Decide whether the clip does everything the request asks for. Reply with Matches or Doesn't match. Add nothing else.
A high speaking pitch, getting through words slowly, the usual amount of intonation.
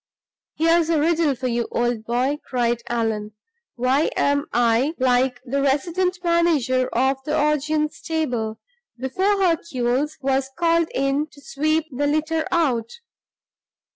Matches